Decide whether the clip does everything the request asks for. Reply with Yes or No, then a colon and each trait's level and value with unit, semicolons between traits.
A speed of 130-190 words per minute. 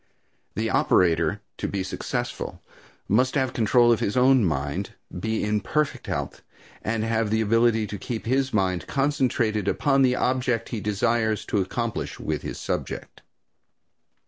Yes: average, 145 wpm